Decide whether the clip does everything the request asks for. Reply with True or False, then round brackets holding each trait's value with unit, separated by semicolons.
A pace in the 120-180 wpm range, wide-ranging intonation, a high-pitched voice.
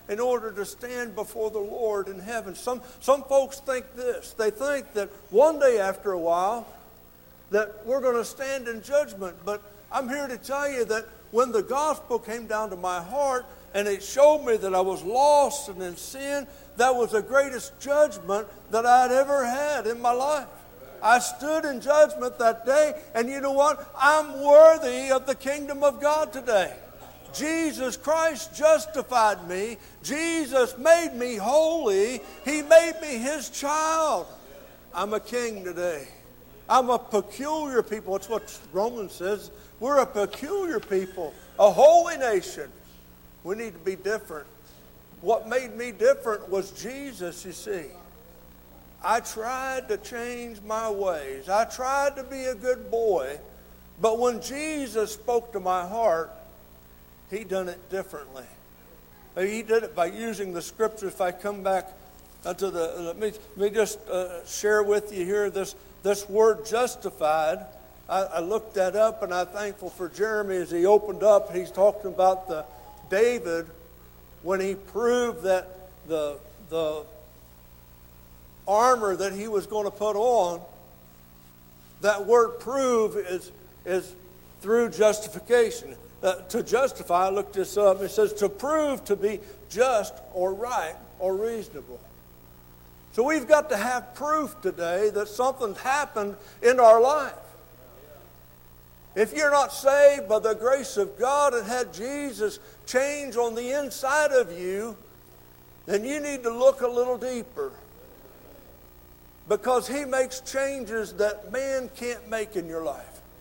True (150 wpm; 6.0 semitones; 220 Hz)